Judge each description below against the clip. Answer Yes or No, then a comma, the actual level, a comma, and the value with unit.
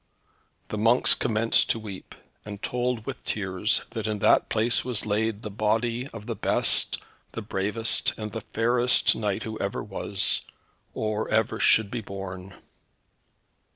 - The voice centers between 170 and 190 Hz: No, low, 110 Hz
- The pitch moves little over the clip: Yes, narrow, 1.9 semitones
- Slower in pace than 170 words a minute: Yes, average, 150 wpm